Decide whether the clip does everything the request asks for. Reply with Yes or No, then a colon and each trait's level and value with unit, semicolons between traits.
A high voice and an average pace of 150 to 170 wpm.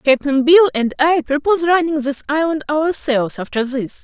Yes: very high, 290 Hz; average, 165 wpm